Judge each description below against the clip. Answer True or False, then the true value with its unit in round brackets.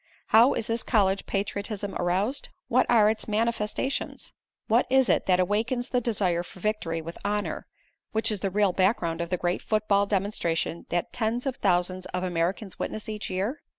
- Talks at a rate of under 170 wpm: False (175 wpm)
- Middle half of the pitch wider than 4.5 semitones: False (3.5 semitones)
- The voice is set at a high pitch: True (205 Hz)